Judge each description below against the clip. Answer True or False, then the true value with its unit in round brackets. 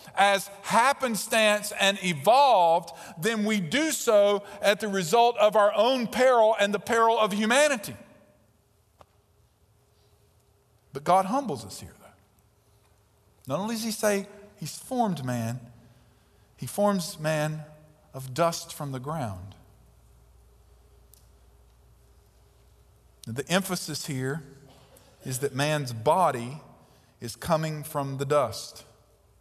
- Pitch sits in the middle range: True (150 Hz)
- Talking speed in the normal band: False (110 wpm)